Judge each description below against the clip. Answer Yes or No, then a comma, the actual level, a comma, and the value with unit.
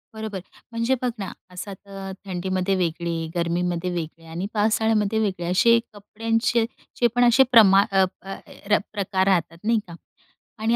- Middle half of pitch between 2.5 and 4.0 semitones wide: Yes, average, 3.6 semitones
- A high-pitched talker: Yes, high, 195 Hz